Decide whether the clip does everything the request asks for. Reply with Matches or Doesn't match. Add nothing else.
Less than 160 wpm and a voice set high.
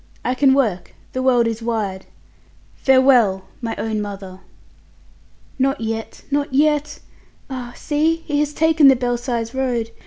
Matches